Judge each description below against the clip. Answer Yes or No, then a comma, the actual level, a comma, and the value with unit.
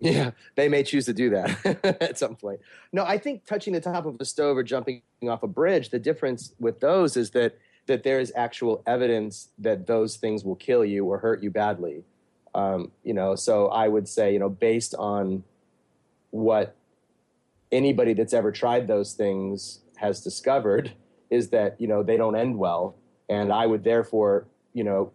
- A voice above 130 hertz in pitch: No, low, 115 Hz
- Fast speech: No, average, 190 wpm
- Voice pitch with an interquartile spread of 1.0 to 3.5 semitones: No, average, 4.4 semitones